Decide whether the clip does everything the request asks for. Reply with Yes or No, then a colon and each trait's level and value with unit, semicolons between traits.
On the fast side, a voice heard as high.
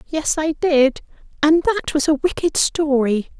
No: average, 160 wpm; very high, 300 Hz